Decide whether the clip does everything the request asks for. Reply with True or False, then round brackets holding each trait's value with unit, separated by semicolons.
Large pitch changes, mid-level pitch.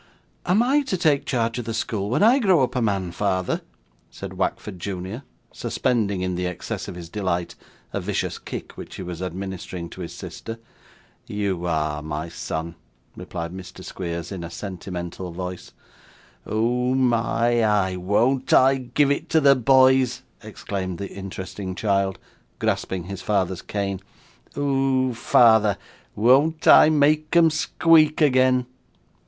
False (6.1 semitones; 105 Hz)